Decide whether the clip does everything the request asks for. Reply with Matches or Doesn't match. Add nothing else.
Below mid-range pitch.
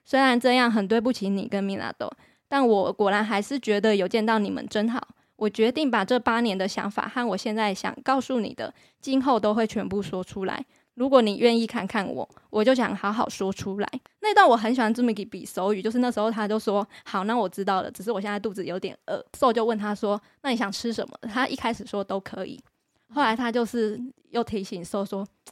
Doesn't match